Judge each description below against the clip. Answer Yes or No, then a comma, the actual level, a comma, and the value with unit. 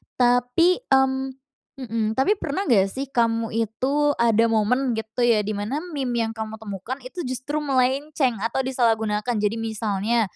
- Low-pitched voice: No, high, 240 Hz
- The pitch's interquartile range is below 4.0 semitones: Yes, average, 3.2 semitones